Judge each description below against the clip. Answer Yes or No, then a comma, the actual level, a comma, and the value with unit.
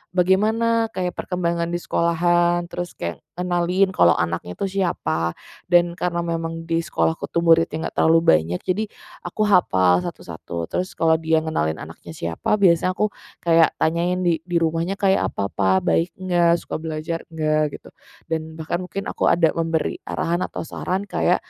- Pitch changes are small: Yes, narrow, 2.2 semitones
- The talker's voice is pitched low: No, medium, 170 Hz